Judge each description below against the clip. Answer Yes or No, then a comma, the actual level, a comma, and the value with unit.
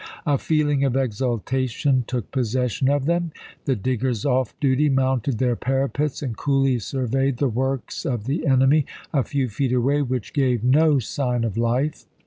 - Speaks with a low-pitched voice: Yes, low, 130 Hz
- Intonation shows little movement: Yes, narrow, 2.1 semitones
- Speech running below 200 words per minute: Yes, average, 160 wpm